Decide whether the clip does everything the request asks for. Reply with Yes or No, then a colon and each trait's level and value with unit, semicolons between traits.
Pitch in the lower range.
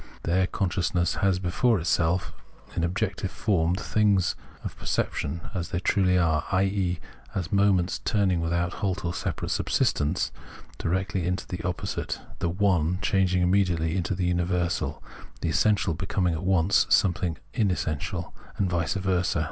Yes: very low, 90 Hz